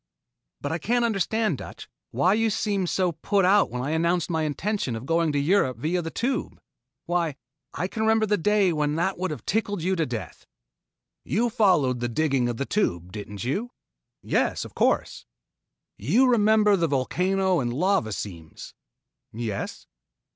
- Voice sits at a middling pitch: Yes, medium, 170 Hz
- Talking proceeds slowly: No, average, 170 wpm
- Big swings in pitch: Yes, wide, 7.3 semitones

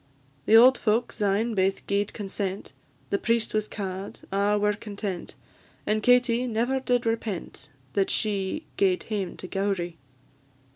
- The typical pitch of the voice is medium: No, high, 205 Hz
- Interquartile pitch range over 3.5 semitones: No, average, 2.8 semitones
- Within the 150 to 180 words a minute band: No, average, 140 wpm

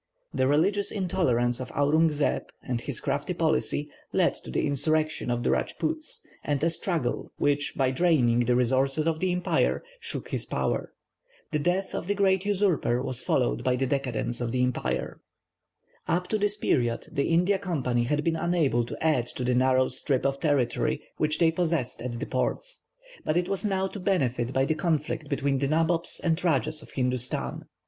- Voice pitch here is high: No, medium, 150 Hz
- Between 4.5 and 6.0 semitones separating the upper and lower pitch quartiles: Yes, wide, 5.4 semitones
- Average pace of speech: Yes, average, 185 wpm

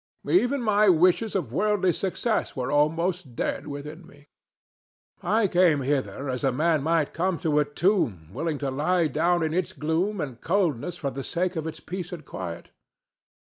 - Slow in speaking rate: No, average, 170 wpm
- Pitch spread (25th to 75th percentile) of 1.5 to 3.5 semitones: No, average, 4.2 semitones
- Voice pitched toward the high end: No, medium, 160 Hz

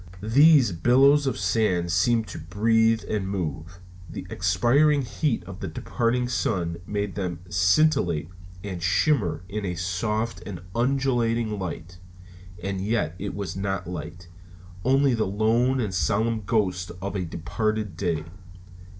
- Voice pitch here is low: Yes, low, 100 Hz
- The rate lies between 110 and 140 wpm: Yes, slow, 135 wpm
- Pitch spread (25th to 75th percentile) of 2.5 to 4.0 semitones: No, average, 4.5 semitones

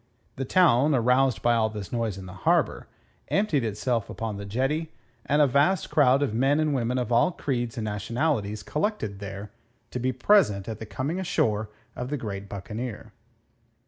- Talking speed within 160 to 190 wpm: Yes, average, 175 wpm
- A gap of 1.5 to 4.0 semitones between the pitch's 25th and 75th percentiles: No, average, 5.1 semitones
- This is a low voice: Yes, low, 120 Hz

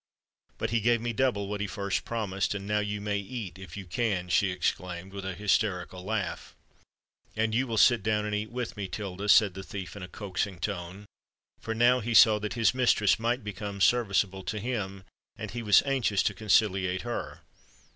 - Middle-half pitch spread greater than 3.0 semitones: No, narrow, 2.6 semitones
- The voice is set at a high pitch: No, low, 105 Hz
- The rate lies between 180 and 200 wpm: Yes, average, 190 wpm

